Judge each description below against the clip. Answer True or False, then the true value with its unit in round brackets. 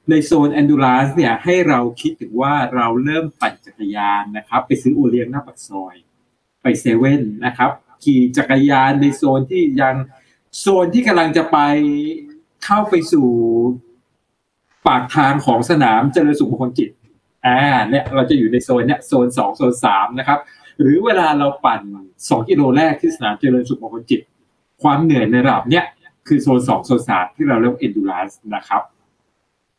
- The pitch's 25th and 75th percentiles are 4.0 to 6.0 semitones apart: True (4.4 semitones)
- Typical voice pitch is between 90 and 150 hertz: True (135 Hz)